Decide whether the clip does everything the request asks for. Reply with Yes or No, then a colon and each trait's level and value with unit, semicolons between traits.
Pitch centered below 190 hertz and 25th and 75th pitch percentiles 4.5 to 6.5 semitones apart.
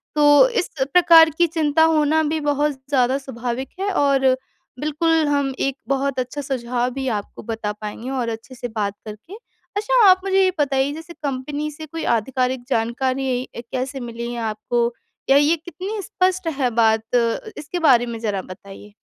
No: very high, 270 Hz; average, 4.8 semitones